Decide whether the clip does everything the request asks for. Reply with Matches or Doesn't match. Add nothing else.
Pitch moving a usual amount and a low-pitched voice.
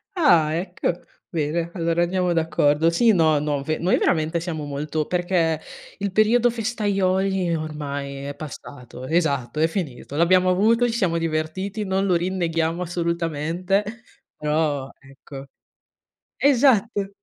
Doesn't match